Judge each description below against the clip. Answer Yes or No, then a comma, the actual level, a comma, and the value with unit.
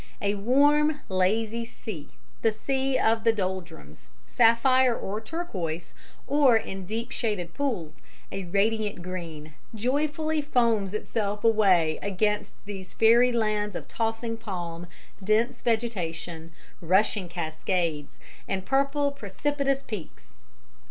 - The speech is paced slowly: Yes, slow, 110 wpm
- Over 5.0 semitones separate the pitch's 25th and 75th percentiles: No, average, 4.7 semitones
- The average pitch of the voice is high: Yes, high, 215 Hz